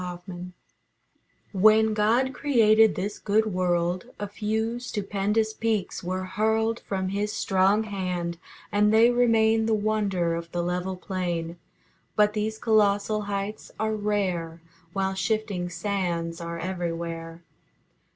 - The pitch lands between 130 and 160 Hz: No, high, 200 Hz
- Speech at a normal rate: No, slow, 120 wpm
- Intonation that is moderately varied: Yes, average, 3.4 semitones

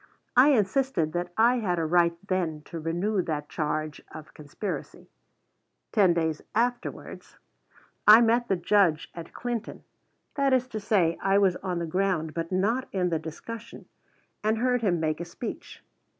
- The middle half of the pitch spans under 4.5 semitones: No, wide, 5.5 semitones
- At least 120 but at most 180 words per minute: Yes, average, 160 wpm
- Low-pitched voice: No, medium, 185 Hz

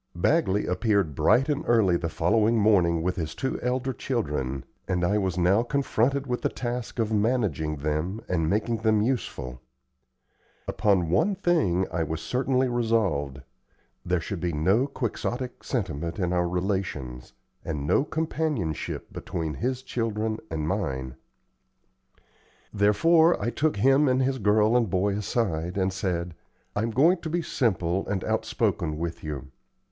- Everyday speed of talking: Yes, average, 145 wpm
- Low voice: Yes, low, 100 Hz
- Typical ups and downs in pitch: No, wide, 6.4 semitones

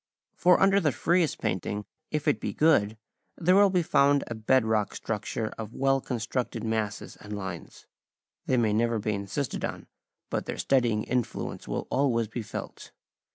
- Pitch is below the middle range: Yes, low, 120 Hz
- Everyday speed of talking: Yes, average, 165 wpm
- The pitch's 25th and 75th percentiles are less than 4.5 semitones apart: No, average, 4.9 semitones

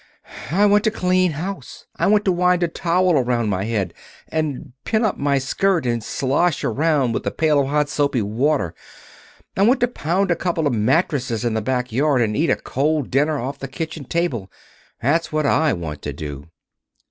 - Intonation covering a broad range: Yes, wide, 6.0 semitones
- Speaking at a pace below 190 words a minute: No, average, 195 wpm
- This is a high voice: No, medium, 145 Hz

